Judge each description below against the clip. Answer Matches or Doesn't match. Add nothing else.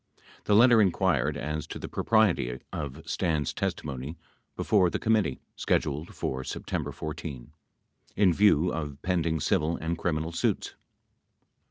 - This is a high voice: Doesn't match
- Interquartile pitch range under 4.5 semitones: Matches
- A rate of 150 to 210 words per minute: Doesn't match